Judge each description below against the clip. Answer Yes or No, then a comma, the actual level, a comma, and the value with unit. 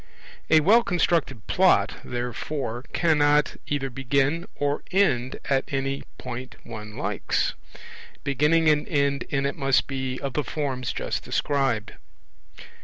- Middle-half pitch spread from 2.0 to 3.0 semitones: Yes, narrow, 2.6 semitones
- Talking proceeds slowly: Yes, slow, 125 wpm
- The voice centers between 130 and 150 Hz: Yes, medium, 140 Hz